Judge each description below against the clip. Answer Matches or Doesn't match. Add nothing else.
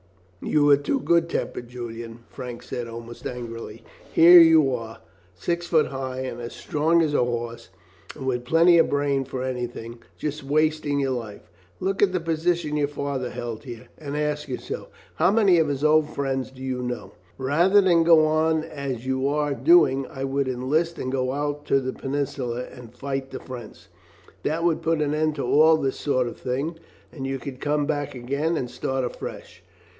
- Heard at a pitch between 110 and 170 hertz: Matches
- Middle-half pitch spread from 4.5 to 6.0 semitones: Doesn't match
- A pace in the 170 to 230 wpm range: Matches